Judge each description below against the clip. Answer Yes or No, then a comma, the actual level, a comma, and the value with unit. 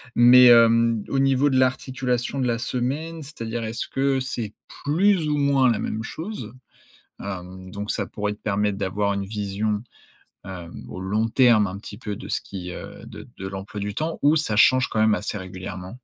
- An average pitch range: Yes, average, 4.5 semitones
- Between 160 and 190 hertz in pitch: No, low, 115 Hz